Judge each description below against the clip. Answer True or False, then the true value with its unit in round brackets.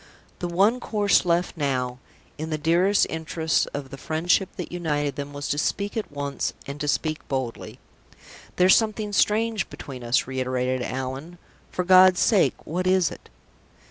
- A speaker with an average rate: True (160 wpm)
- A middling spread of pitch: True (5.0 semitones)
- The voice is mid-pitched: True (160 Hz)